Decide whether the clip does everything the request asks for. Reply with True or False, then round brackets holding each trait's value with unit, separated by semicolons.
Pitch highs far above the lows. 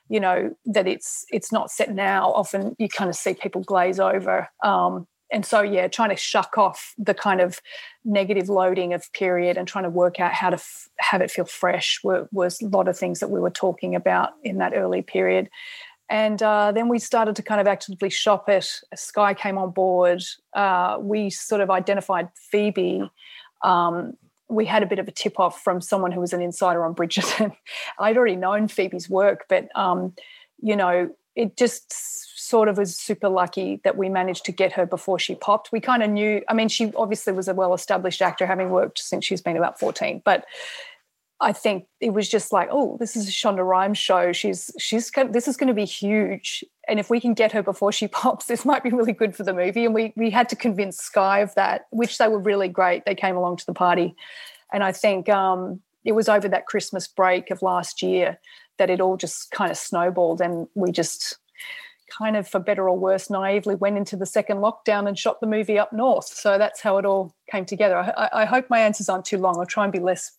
False (2.8 semitones)